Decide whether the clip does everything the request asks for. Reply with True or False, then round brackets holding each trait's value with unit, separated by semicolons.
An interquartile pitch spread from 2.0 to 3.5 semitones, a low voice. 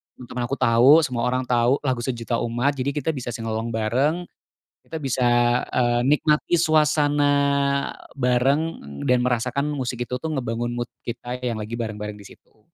True (2.8 semitones; 125 Hz)